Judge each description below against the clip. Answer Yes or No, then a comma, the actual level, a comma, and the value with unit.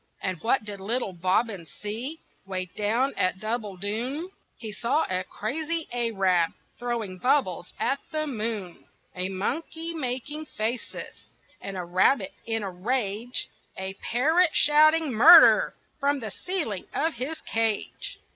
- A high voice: Yes, high, 230 Hz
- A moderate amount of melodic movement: No, wide, 6.9 semitones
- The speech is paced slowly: Yes, slow, 130 wpm